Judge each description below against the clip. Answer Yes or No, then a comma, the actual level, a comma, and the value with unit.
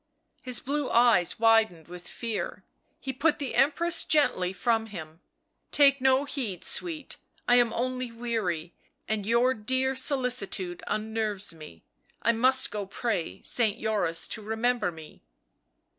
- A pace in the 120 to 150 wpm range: Yes, average, 145 wpm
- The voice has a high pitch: Yes, high, 230 Hz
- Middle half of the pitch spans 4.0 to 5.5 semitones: Yes, average, 4.9 semitones